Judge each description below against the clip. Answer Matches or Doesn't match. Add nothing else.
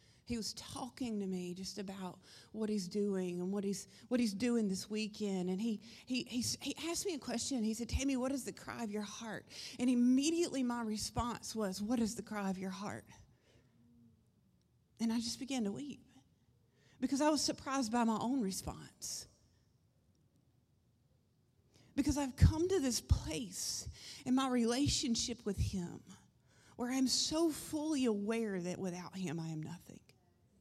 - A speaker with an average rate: Matches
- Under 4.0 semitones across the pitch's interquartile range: Doesn't match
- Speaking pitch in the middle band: Doesn't match